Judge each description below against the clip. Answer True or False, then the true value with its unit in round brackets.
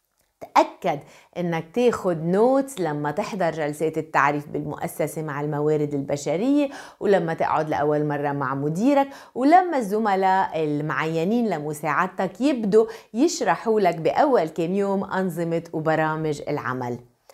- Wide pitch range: True (5.8 semitones)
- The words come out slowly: False (105 wpm)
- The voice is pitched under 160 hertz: False (165 Hz)